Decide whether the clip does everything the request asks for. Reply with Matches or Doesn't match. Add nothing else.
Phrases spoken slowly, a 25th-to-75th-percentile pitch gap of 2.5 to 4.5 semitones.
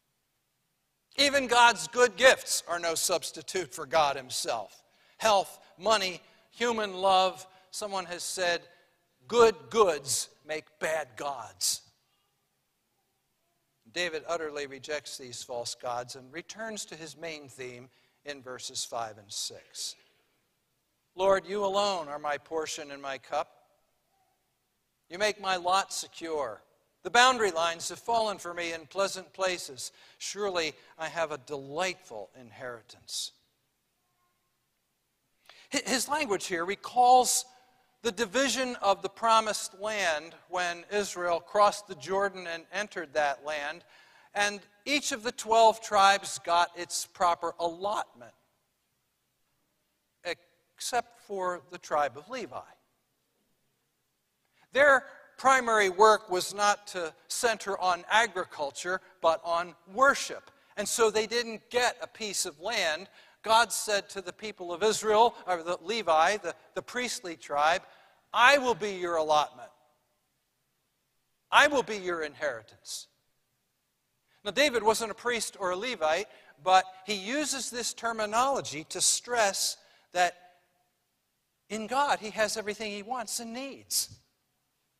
Doesn't match